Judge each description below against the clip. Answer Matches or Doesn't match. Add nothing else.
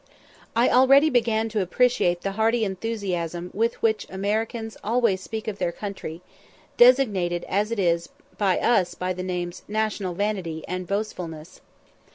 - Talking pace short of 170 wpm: Matches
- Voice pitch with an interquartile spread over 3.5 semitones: Matches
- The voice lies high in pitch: Matches